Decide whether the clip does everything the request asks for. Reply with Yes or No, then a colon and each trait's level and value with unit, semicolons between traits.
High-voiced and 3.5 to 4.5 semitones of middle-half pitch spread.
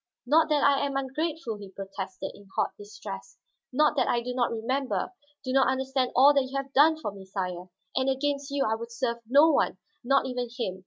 Yes: very high, 260 Hz; average, 4.1 semitones